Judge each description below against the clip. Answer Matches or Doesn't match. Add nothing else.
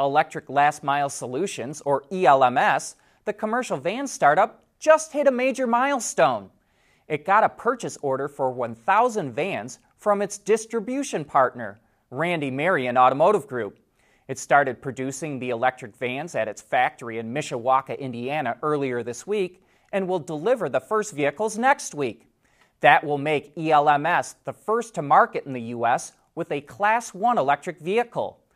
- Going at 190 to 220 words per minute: Doesn't match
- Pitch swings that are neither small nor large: Doesn't match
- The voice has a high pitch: Doesn't match